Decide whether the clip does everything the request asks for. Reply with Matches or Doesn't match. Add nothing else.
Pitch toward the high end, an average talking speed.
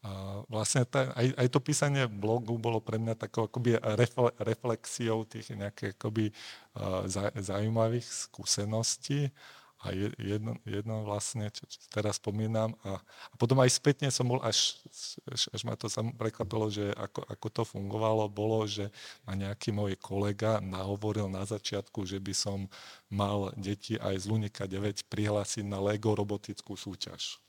Doesn't match